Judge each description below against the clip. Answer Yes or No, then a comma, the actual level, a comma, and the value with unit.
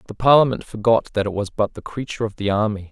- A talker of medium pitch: No, low, 110 Hz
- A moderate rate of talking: No, fast, 245 wpm